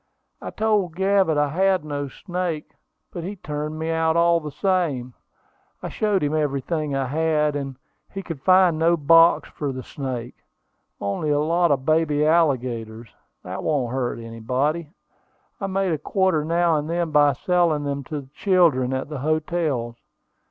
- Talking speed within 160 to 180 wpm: Yes, average, 165 wpm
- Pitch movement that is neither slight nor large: Yes, average, 3.6 semitones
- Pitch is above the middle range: No, medium, 155 Hz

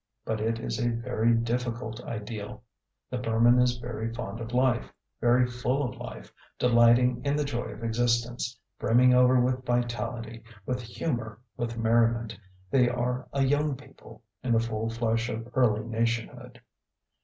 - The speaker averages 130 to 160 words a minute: Yes, average, 155 wpm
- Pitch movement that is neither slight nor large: No, narrow, 1.4 semitones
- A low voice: Yes, low, 120 Hz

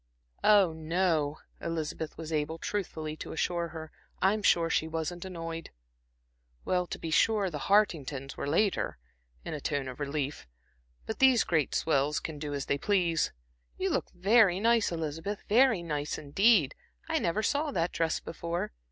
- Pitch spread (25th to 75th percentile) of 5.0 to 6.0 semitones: No, average, 4.2 semitones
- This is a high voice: No, medium, 165 Hz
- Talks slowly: No, average, 160 wpm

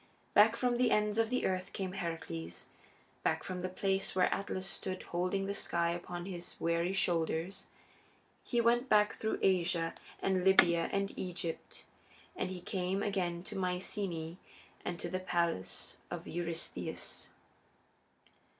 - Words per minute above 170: No, average, 140 wpm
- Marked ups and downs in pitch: No, narrow, 2.4 semitones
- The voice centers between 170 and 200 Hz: Yes, medium, 185 Hz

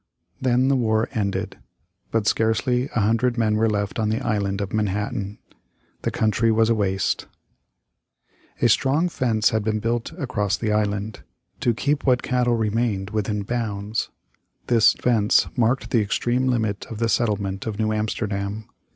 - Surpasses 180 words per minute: No, average, 155 wpm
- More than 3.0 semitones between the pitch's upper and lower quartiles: No, narrow, 2.4 semitones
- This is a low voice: Yes, low, 110 Hz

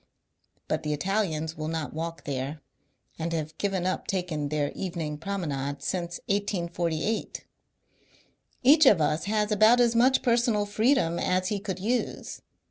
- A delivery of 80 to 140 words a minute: Yes, slow, 135 wpm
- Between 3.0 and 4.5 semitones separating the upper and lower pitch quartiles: No, average, 5.0 semitones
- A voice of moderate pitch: Yes, medium, 180 Hz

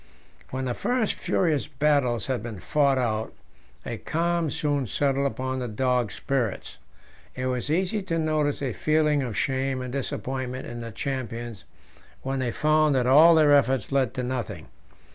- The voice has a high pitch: No, low, 135 Hz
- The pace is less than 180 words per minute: Yes, average, 160 wpm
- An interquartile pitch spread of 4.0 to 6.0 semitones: No, average, 3.3 semitones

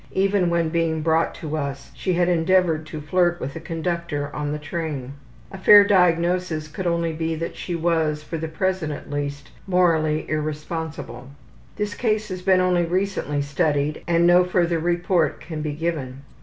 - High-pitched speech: No, medium, 165 Hz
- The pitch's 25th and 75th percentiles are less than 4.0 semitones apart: Yes, average, 2.7 semitones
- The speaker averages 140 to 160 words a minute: No, average, 170 wpm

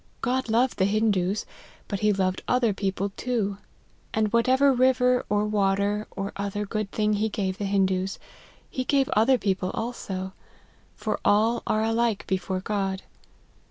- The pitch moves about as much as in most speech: Yes, average, 3.1 semitones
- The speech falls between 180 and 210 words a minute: No, average, 155 wpm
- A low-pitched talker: No, high, 210 Hz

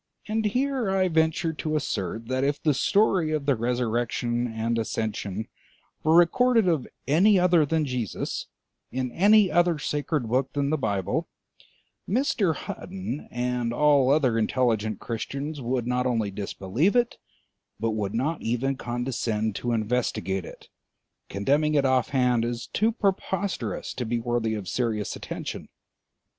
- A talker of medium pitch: No, low, 130 Hz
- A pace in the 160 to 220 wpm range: No, average, 140 wpm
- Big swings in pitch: Yes, wide, 5.9 semitones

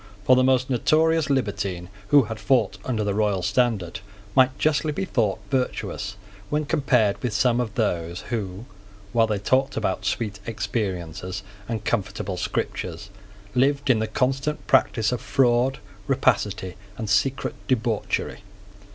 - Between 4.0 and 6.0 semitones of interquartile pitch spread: Yes, average, 4.5 semitones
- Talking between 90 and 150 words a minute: Yes, average, 140 wpm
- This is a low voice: Yes, low, 115 Hz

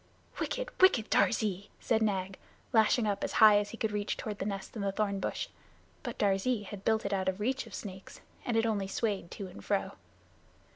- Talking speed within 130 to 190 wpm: No, fast, 205 wpm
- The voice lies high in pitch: Yes, high, 205 Hz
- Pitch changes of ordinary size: No, narrow, 2.2 semitones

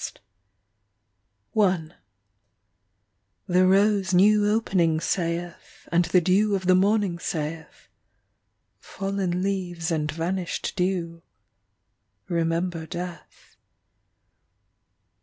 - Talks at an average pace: No, slow, 80 wpm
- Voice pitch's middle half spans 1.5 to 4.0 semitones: Yes, narrow, 2.5 semitones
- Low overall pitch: No, medium, 180 Hz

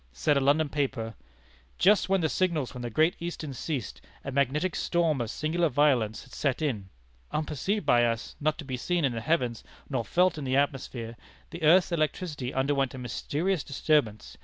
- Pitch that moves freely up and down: No, average, 4.4 semitones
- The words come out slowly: No, average, 185 wpm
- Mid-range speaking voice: Yes, medium, 145 Hz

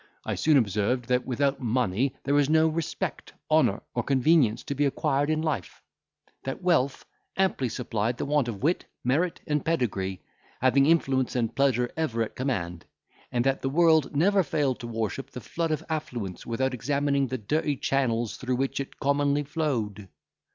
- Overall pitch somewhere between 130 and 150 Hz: Yes, low, 135 Hz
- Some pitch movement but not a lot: Yes, average, 3.7 semitones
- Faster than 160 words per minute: Yes, average, 170 wpm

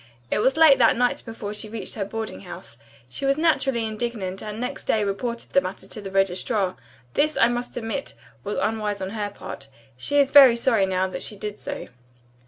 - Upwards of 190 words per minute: Yes, average, 200 wpm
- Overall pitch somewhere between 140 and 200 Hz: No, high, 220 Hz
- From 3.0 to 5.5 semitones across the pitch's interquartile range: Yes, average, 3.9 semitones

